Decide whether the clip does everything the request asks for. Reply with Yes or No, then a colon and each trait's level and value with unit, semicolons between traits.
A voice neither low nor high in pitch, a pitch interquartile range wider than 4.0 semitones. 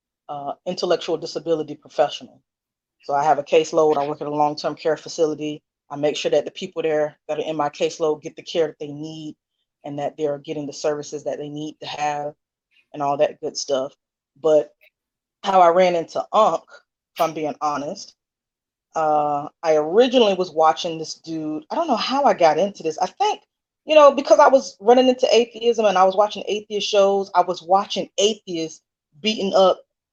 Yes: medium, 160 Hz; average, 4.6 semitones